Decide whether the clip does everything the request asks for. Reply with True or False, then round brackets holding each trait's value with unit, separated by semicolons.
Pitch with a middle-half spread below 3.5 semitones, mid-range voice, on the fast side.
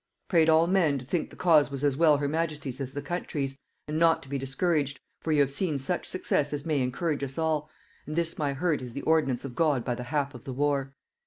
True (2.9 semitones; 145 Hz; 245 wpm)